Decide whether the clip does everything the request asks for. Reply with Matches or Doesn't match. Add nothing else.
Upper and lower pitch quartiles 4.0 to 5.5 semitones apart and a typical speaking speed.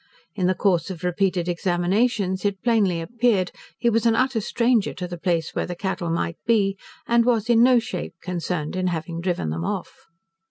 Matches